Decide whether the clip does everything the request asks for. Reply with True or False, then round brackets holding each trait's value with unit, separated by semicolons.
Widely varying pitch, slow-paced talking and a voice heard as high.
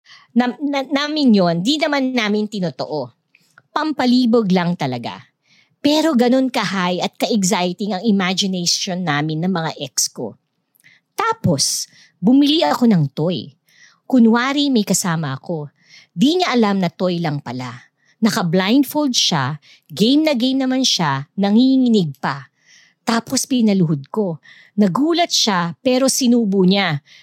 True (6.9 semitones; 125 wpm; 210 Hz)